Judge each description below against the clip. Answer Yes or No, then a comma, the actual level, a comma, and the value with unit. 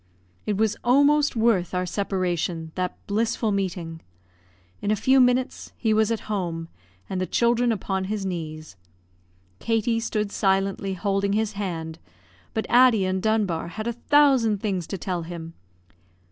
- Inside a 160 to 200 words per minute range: No, average, 145 wpm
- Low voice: No, high, 200 Hz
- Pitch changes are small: No, average, 3.7 semitones